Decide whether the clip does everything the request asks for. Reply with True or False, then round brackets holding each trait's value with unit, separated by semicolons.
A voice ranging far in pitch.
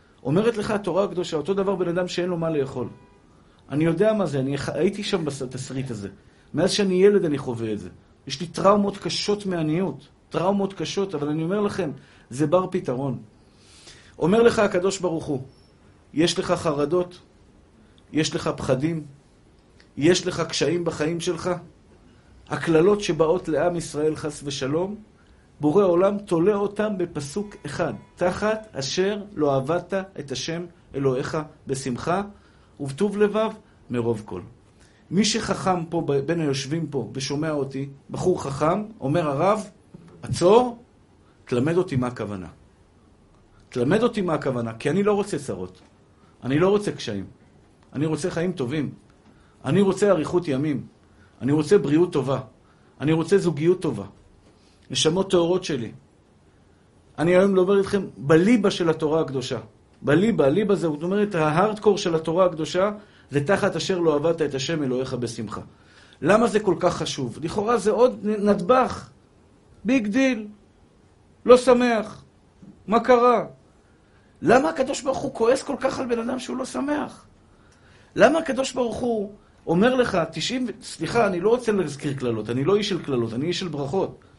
True (6.9 semitones)